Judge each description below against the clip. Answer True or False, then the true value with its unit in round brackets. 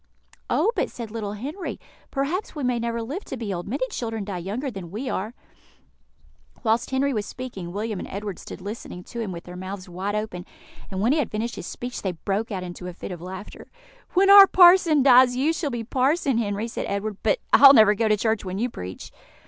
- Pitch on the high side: True (220 Hz)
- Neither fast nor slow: False (220 wpm)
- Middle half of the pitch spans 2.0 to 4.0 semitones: False (4.8 semitones)